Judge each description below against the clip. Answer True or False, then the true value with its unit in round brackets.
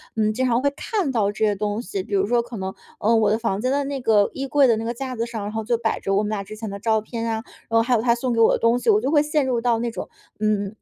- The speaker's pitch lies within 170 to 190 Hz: False (230 Hz)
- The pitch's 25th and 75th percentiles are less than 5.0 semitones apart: True (2.6 semitones)